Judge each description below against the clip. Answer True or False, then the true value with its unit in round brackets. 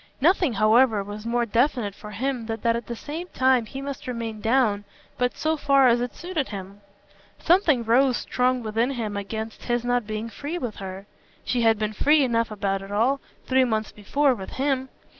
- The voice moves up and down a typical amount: True (3.6 semitones)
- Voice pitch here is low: False (235 Hz)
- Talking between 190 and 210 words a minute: True (195 wpm)